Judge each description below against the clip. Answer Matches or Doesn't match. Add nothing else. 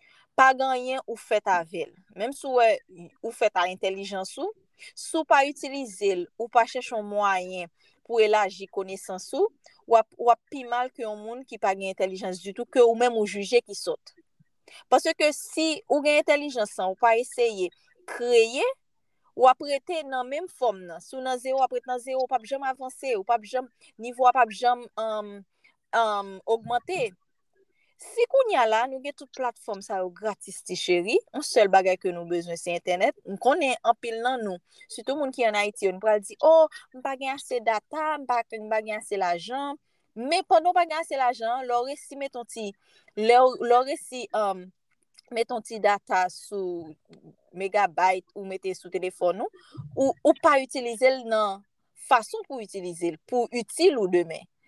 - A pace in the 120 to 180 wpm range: Matches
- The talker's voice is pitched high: Matches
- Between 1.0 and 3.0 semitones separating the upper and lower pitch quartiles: Doesn't match